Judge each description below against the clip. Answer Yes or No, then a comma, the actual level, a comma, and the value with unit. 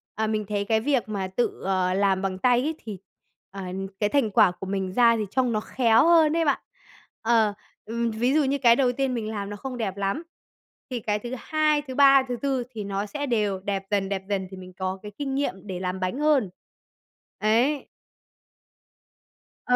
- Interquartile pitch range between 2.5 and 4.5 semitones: No, average, 4.9 semitones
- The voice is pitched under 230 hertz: Yes, high, 220 Hz